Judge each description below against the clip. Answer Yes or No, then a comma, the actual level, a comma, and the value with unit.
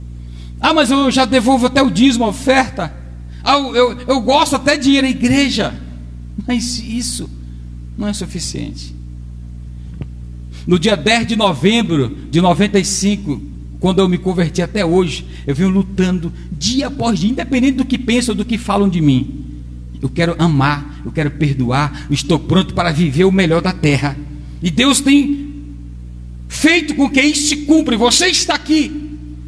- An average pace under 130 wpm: No, average, 165 wpm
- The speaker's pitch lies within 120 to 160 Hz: No, medium, 185 Hz